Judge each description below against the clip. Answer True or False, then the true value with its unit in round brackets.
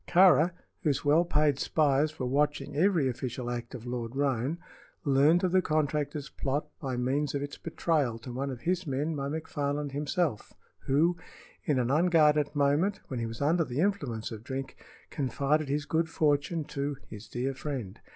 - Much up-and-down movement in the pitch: False (2.9 semitones)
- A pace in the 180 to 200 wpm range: False (170 wpm)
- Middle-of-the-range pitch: True (145 Hz)